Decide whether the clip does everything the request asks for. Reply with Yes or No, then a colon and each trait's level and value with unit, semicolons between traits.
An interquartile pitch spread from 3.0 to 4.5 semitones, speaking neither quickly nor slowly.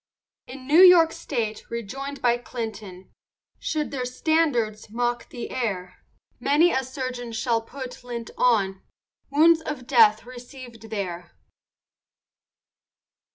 No: average, 3.6 semitones; slow, 110 wpm